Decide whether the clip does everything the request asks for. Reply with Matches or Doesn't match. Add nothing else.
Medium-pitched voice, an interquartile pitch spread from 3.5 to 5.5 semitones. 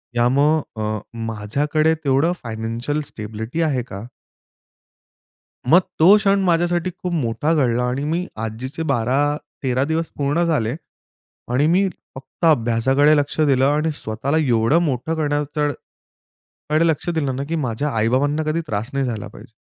Matches